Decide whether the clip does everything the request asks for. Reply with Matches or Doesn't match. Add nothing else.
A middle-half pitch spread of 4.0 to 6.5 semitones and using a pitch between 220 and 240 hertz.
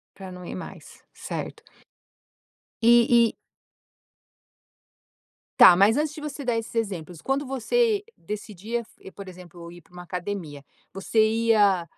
Doesn't match